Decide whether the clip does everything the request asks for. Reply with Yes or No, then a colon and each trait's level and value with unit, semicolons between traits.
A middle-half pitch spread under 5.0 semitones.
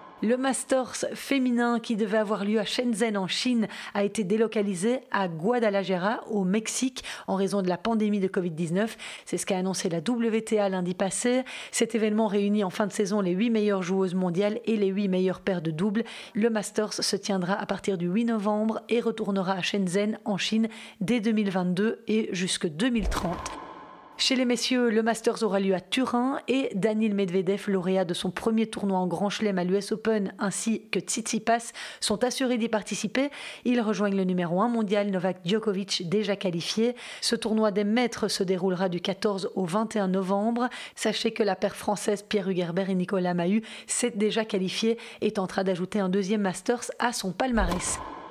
Yes: average, 2.8 semitones